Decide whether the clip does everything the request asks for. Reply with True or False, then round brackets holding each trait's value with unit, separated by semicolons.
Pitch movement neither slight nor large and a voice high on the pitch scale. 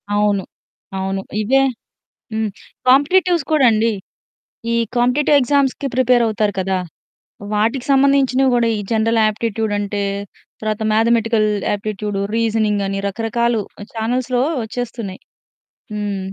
True (3.3 semitones; 225 Hz)